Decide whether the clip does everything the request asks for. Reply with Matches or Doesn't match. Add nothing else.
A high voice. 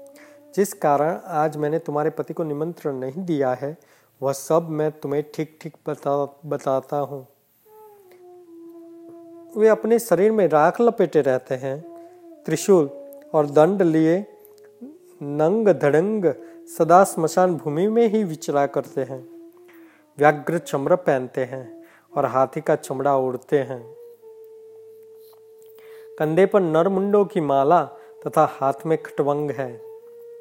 Doesn't match